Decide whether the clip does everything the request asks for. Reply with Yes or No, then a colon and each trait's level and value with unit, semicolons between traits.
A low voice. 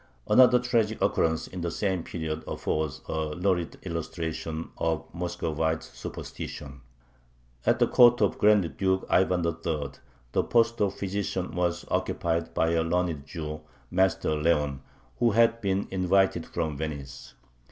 Yes: very low, 85 Hz